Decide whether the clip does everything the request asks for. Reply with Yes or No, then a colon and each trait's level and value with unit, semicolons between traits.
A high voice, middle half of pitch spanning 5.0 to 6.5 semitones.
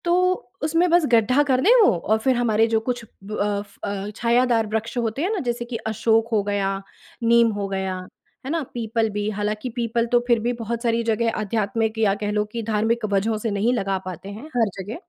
No: high, 225 Hz; narrow, 2.4 semitones